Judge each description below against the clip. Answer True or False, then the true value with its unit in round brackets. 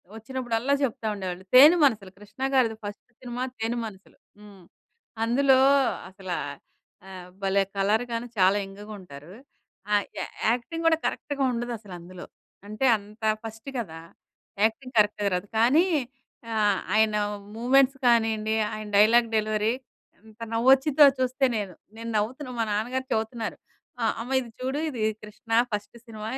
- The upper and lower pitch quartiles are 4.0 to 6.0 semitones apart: False (3.3 semitones)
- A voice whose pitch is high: True (220 Hz)